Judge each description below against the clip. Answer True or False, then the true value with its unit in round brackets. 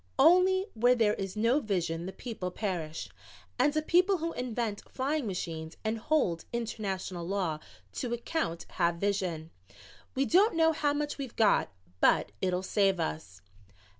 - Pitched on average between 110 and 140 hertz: False (215 Hz)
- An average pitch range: False (7.9 semitones)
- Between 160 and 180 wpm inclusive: False (150 wpm)